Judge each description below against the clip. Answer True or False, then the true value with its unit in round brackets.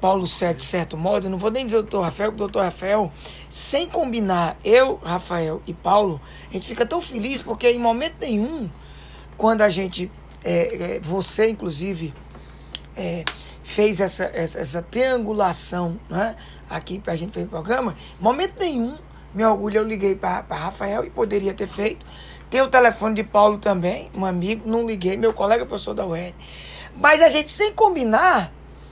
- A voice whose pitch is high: True (205 Hz)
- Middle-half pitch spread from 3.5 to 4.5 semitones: True (4.1 semitones)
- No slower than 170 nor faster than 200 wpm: True (175 wpm)